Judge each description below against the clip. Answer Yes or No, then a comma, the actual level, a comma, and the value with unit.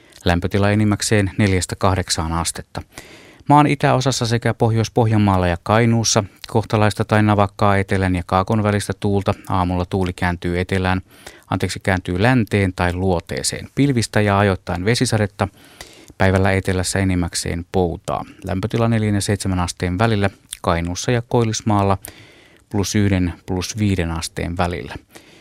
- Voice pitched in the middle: No, low, 100 Hz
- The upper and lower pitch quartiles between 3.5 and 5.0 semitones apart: No, average, 3.0 semitones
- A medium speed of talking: Yes, average, 115 wpm